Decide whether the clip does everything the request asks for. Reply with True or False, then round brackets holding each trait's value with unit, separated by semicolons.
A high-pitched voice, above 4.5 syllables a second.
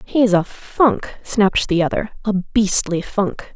False (200 Hz; 3.7 syllables/s)